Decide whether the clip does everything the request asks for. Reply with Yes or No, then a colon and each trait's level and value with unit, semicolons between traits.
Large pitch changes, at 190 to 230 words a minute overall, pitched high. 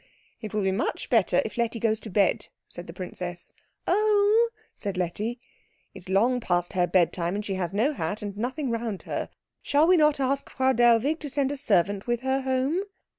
Yes: wide, 5.8 semitones; average, 200 wpm; high, 230 Hz